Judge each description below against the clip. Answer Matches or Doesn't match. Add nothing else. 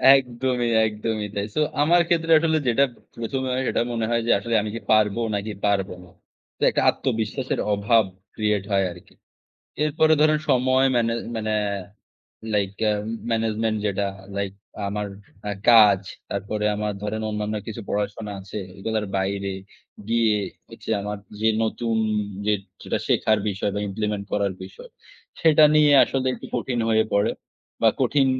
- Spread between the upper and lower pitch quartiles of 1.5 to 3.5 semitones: Matches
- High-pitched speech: Doesn't match